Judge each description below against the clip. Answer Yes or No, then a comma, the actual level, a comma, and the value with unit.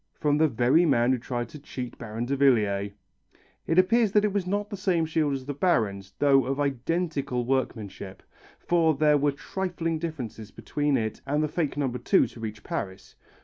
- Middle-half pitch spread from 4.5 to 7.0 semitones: Yes, average, 5.3 semitones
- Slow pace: No, average, 180 wpm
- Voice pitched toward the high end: No, medium, 140 Hz